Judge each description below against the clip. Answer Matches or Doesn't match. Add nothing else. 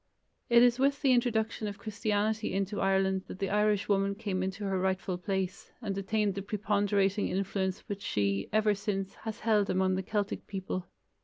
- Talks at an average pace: Matches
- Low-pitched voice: Doesn't match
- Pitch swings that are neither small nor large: Doesn't match